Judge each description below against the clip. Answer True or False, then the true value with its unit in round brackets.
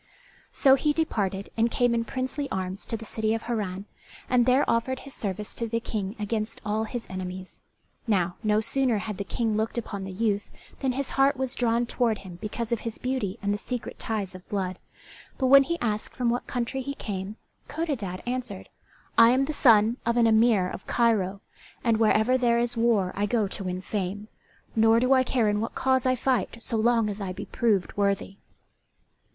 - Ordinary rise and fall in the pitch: True (3.4 semitones)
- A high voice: True (225 Hz)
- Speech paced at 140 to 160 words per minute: False (200 wpm)